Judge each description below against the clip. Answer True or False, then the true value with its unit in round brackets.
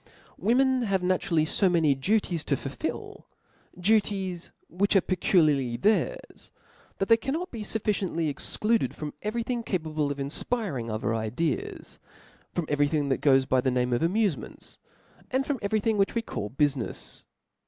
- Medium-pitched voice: True (180 Hz)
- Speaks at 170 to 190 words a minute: False (155 wpm)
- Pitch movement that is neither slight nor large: False (7.3 semitones)